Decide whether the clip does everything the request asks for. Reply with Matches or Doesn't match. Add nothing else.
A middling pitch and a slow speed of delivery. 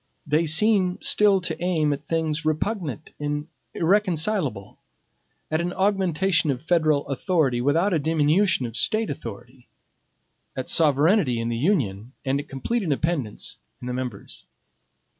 Matches